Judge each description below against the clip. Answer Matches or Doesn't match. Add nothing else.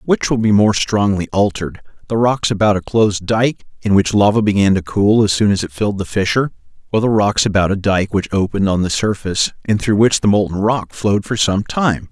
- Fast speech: Matches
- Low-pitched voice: Matches